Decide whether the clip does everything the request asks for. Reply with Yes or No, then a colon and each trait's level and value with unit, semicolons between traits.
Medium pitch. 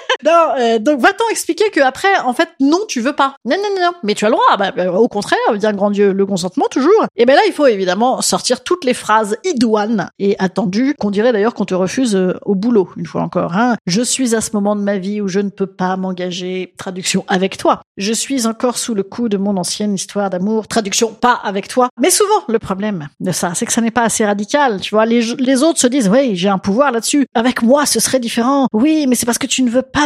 No: high, 230 Hz